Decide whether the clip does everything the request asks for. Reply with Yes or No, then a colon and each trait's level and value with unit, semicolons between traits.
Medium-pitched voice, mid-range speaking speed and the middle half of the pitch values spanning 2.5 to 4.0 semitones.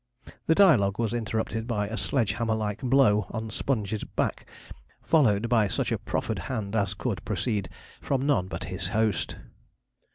No: low, 110 Hz; average, 160 wpm; average, 3.0 semitones